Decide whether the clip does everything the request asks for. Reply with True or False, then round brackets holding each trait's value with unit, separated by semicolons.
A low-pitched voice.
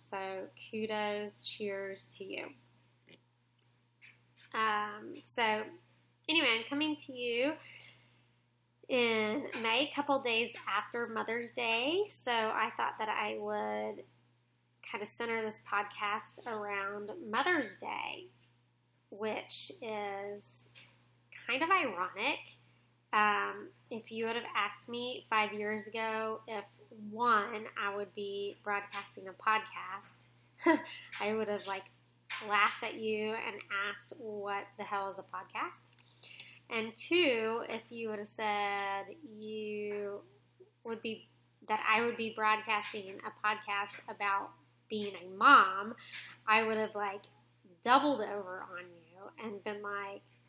False (210 Hz)